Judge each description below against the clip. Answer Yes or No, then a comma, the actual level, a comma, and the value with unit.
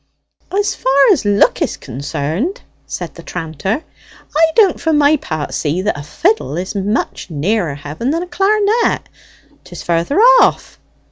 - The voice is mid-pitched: No, high, 225 Hz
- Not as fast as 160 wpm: Yes, average, 150 wpm